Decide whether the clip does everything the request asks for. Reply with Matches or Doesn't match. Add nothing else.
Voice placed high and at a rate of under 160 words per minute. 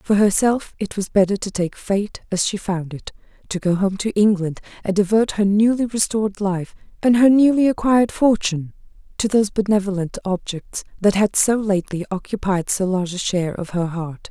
Doesn't match